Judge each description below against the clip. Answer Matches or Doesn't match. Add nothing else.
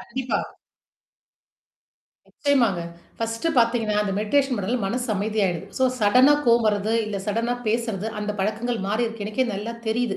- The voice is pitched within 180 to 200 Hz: Doesn't match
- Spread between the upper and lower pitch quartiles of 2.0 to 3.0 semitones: Matches